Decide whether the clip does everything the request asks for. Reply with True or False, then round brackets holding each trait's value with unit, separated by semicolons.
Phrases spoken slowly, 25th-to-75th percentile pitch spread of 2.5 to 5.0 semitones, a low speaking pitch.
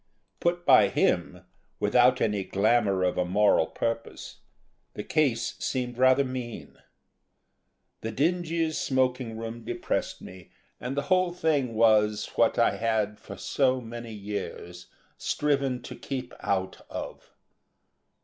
True (125 wpm; 4.3 semitones; 120 Hz)